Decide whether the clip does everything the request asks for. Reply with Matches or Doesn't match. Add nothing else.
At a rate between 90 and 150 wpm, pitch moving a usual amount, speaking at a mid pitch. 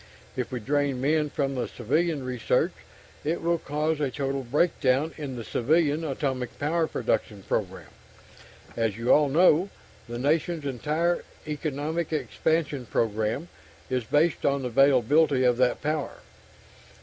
Matches